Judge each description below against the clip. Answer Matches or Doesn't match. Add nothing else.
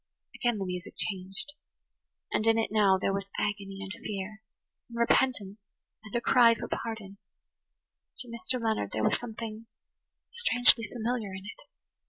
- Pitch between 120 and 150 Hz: Doesn't match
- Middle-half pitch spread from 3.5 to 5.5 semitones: Doesn't match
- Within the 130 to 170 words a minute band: Matches